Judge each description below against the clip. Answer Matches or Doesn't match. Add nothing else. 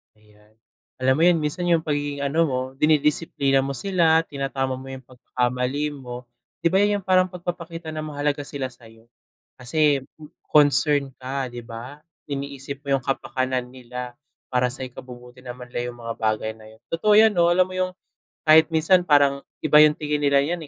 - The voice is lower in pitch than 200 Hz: Matches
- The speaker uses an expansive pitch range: Doesn't match